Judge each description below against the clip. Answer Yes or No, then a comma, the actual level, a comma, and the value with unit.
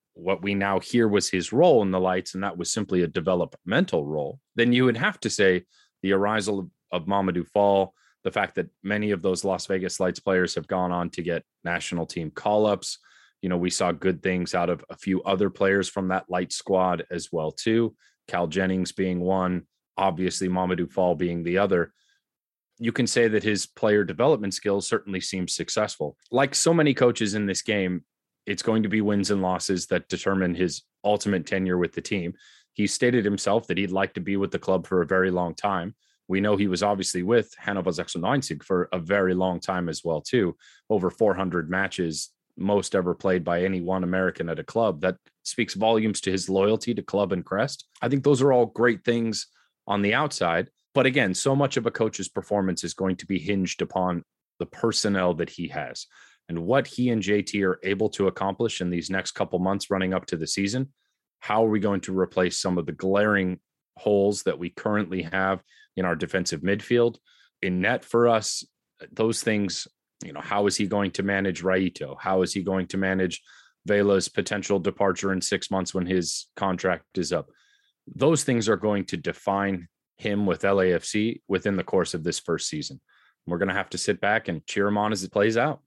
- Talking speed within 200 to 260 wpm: Yes, fast, 205 wpm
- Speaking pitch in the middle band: No, very low, 95 Hz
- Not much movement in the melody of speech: Yes, narrow, 2.2 semitones